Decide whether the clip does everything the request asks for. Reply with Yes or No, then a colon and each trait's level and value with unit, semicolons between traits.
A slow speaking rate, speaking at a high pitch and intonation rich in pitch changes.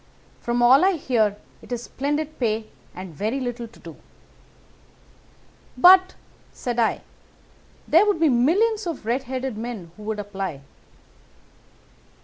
Yes: slow, 130 wpm; high, 245 Hz; wide, 5.9 semitones